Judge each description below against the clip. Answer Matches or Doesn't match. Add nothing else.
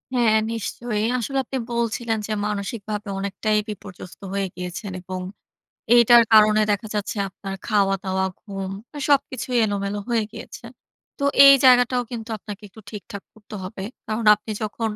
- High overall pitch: Matches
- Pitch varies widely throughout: Doesn't match